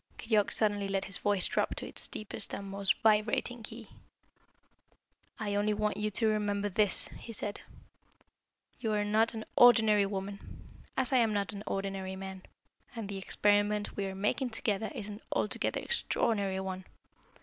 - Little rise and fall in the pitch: Yes, narrow, 1.7 semitones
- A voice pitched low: No, high, 205 Hz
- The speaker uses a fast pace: No, average, 160 wpm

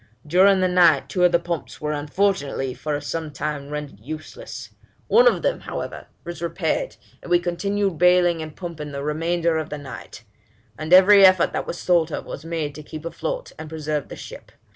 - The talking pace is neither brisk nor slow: Yes, average, 190 wpm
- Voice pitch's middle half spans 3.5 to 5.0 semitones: No, average, 3.1 semitones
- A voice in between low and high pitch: Yes, medium, 165 Hz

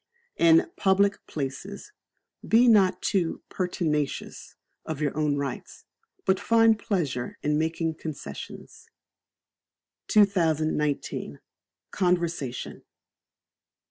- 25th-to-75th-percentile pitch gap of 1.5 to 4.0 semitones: No, average, 5.0 semitones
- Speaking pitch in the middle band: Yes, medium, 170 Hz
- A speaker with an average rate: No, slow, 80 wpm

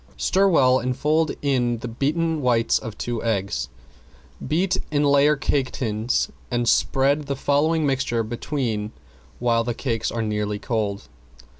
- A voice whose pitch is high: No, low, 125 Hz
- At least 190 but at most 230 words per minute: No, average, 145 wpm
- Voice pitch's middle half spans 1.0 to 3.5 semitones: No, average, 4.1 semitones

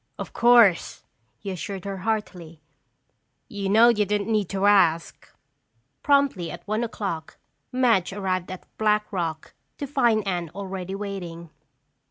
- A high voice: Yes, high, 200 Hz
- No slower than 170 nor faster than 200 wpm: No, slow, 135 wpm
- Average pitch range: Yes, average, 3.1 semitones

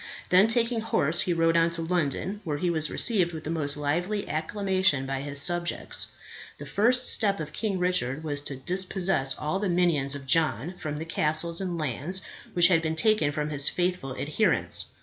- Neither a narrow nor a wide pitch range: Yes, average, 4.0 semitones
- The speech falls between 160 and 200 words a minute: Yes, average, 190 wpm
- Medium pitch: Yes, medium, 165 Hz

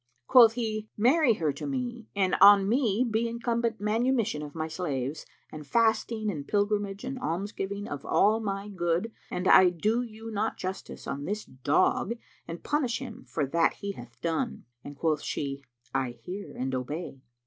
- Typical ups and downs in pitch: No, wide, 6.0 semitones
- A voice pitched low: No, high, 200 Hz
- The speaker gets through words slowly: No, average, 170 wpm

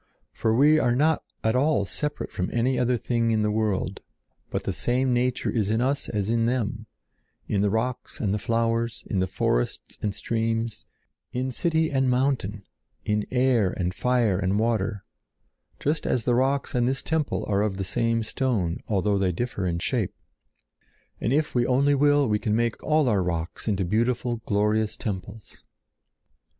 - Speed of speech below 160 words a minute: No, average, 170 wpm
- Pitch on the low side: Yes, low, 115 Hz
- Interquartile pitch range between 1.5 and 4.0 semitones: Yes, average, 3.6 semitones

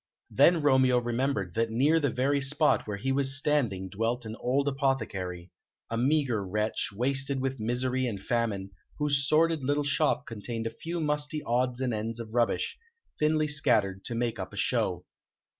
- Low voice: Yes, low, 130 Hz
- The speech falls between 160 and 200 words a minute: Yes, average, 170 wpm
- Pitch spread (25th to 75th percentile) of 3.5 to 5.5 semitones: Yes, average, 3.9 semitones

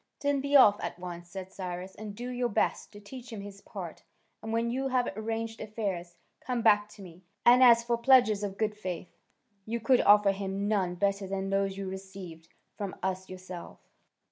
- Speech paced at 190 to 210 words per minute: Yes, average, 195 wpm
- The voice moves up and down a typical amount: Yes, average, 3.3 semitones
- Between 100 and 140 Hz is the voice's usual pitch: No, high, 205 Hz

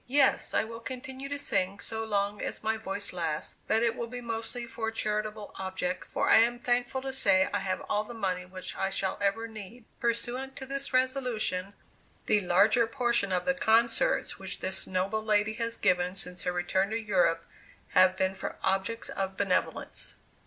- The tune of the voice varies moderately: Yes, average, 3.8 semitones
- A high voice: Yes, high, 215 Hz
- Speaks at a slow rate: No, average, 185 wpm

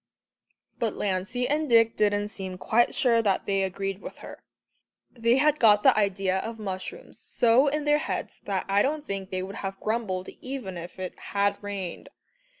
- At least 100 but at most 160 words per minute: No, average, 175 wpm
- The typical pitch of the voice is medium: No, high, 205 Hz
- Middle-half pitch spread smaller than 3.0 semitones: No, average, 3.6 semitones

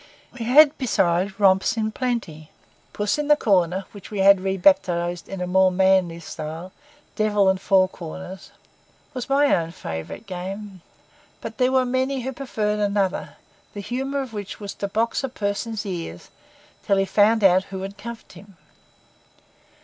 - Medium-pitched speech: No, high, 200 Hz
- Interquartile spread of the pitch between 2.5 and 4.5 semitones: Yes, average, 3.5 semitones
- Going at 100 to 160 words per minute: Yes, average, 155 wpm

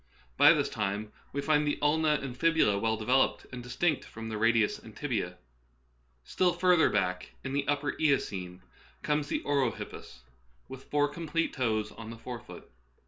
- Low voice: Yes, low, 130 Hz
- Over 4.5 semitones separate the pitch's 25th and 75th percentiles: Yes, average, 5.1 semitones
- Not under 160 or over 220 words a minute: Yes, average, 170 wpm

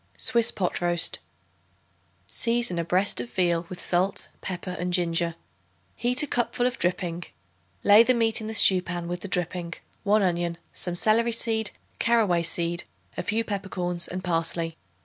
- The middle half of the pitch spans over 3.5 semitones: Yes, average, 4.2 semitones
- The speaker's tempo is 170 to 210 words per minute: No, average, 160 wpm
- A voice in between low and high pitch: Yes, medium, 180 Hz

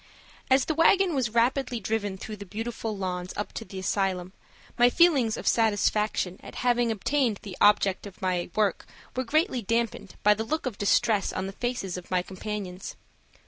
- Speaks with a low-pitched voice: No, high, 215 Hz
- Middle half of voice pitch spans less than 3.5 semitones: No, average, 4.0 semitones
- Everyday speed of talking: Yes, average, 180 wpm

